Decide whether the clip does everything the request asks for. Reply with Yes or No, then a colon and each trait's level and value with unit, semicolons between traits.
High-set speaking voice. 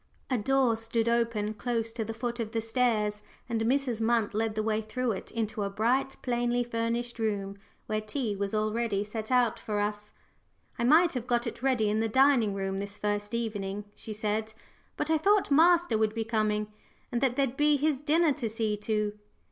Yes: high, 225 Hz